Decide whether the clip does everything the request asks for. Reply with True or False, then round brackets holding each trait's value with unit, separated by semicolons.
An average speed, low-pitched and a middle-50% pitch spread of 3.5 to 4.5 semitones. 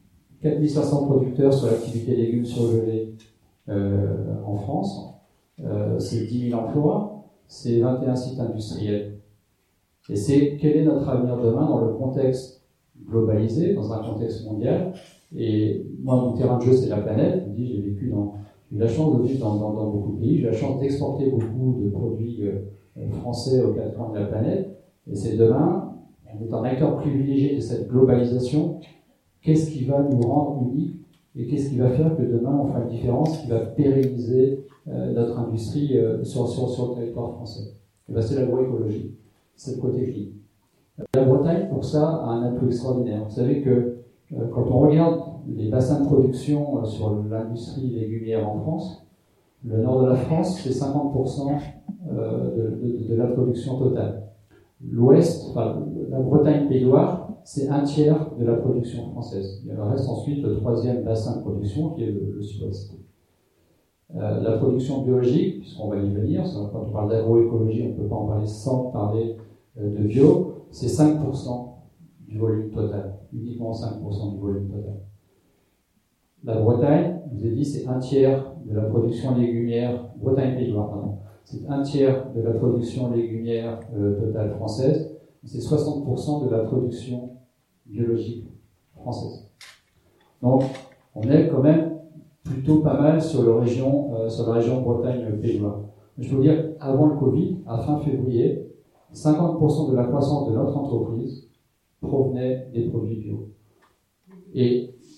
True (160 wpm; 125 Hz; 3.9 semitones)